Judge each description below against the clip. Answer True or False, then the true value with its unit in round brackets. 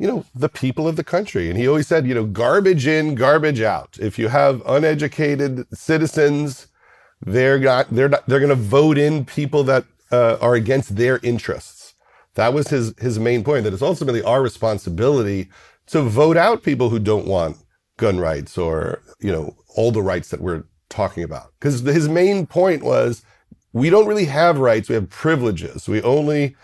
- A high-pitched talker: False (135 Hz)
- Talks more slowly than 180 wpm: False (190 wpm)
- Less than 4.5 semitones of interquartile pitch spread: False (4.8 semitones)